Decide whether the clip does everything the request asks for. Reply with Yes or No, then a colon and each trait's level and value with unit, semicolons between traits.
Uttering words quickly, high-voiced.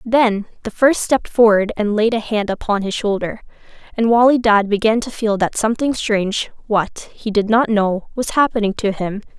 No: average, 180 wpm; high, 220 Hz